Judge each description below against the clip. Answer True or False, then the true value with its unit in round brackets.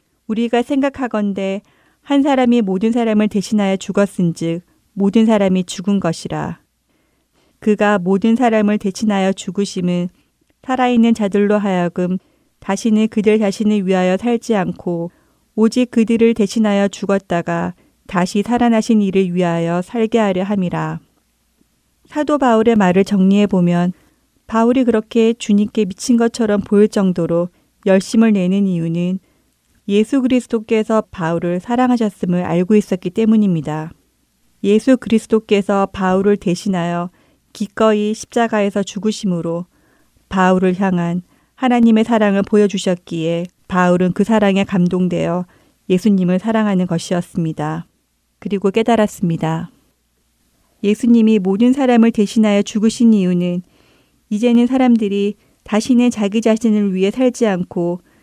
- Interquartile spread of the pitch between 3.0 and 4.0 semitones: True (3.5 semitones)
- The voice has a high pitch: True (205 Hz)